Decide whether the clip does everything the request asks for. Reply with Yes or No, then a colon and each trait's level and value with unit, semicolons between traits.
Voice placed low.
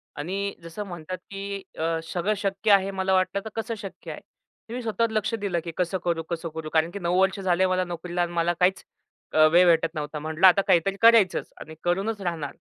No: medium, 185 Hz